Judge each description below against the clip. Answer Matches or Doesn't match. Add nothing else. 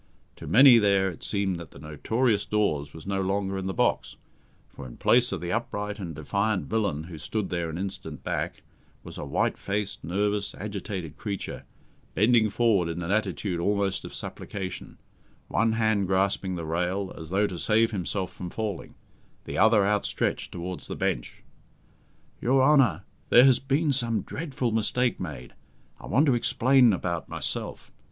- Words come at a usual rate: Matches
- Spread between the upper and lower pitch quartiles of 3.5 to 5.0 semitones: Matches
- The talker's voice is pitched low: Matches